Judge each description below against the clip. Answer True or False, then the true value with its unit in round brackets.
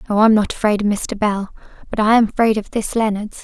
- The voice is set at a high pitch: True (210 Hz)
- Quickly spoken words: True (245 wpm)